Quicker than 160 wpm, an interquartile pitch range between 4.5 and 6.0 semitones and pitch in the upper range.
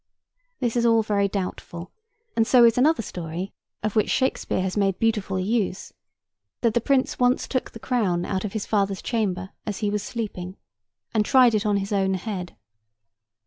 No: average, 180 wpm; average, 3.4 semitones; high, 210 Hz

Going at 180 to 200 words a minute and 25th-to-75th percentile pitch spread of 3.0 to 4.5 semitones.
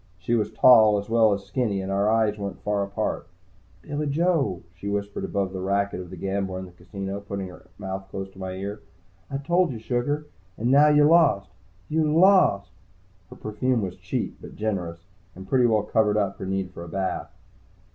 Yes: average, 195 wpm; average, 4.2 semitones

